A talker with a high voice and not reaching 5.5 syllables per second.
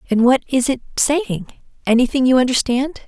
Yes: very high, 260 Hz; 5.0 syllables/s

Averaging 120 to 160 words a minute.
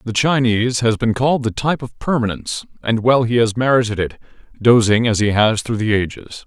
No: fast, 205 wpm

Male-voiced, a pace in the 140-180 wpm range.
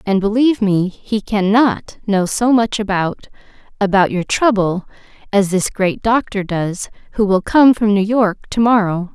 No: female; average, 165 wpm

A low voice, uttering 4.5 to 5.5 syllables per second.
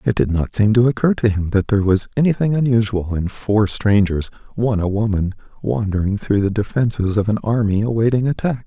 No: low, 110 Hz; 5.7 syllables/s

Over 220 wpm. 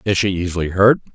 No: fast, 210 wpm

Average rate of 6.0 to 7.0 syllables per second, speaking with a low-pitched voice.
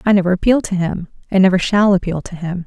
No: 6.4 syllables/s; medium, 185 Hz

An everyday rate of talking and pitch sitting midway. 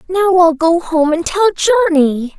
No: average, 175 wpm; very high, 340 Hz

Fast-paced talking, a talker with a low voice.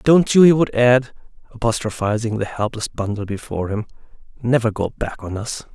No: average, 165 wpm; low, 115 Hz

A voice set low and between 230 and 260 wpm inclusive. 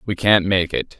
Yes: very low, 95 Hz; fast, 240 wpm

